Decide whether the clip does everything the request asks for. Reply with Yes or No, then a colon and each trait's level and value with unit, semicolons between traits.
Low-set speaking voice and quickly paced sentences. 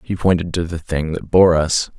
Yes: very low, 85 Hz; fast, 240 wpm